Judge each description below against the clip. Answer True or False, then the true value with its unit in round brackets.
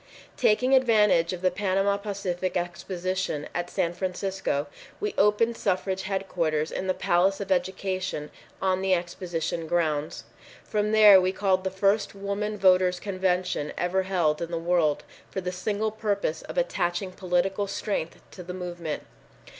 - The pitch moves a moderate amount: False (2.3 semitones)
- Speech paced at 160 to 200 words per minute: False (145 wpm)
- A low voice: False (185 Hz)